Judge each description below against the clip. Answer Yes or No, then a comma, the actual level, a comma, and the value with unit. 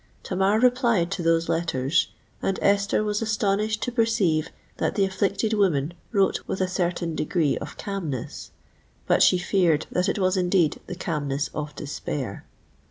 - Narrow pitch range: No, average, 3.7 semitones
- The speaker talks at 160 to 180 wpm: No, average, 150 wpm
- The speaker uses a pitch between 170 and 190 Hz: Yes, medium, 185 Hz